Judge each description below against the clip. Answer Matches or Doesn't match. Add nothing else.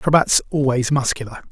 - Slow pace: Matches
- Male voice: Matches